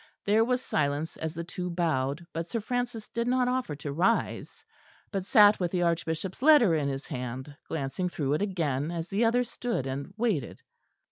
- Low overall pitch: No, medium, 175 Hz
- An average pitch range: No, wide, 7.2 semitones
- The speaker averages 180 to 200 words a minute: Yes, average, 185 wpm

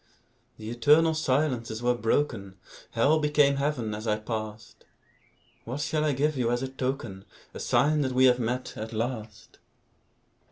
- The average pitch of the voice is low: Yes, low, 125 Hz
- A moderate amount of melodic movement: Yes, average, 4.4 semitones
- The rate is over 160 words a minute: No, average, 155 wpm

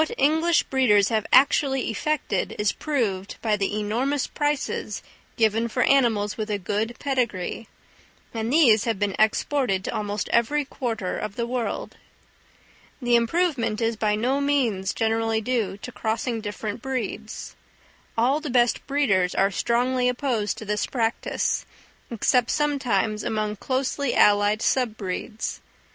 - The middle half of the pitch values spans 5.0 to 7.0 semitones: No, average, 3.9 semitones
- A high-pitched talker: Yes, high, 230 Hz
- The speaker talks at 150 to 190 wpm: No, average, 140 wpm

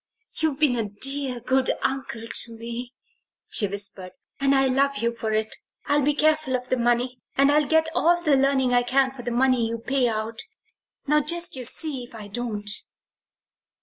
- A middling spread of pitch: Yes, average, 3.1 semitones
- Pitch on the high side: Yes, very high, 255 Hz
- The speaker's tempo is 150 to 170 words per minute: No, average, 185 wpm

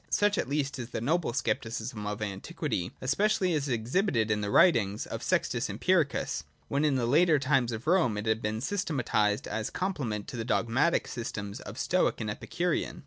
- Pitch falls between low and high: No, low, 120 Hz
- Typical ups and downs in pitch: No, wide, 5.8 semitones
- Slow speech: No, average, 190 wpm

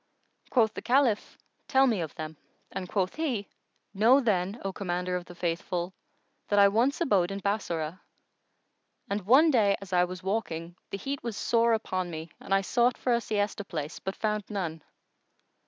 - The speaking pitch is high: Yes, high, 200 Hz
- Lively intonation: No, average, 4.3 semitones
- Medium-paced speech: Yes, average, 175 wpm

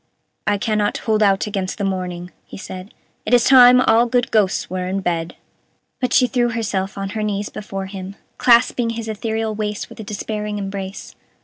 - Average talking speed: Yes, average, 185 wpm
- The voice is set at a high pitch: Yes, high, 210 Hz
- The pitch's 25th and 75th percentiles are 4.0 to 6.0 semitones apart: No, average, 2.7 semitones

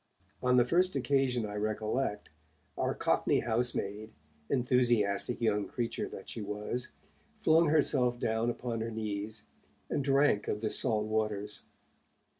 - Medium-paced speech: No, slow, 130 wpm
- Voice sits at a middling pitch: No, low, 115 Hz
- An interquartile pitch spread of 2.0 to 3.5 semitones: Yes, average, 3.0 semitones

